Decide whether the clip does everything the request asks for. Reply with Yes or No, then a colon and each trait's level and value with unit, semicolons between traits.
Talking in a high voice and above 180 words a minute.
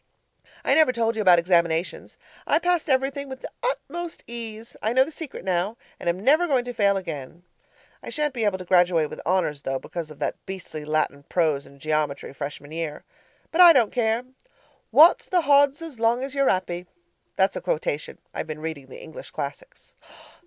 Yes: high, 200 Hz; average, 190 wpm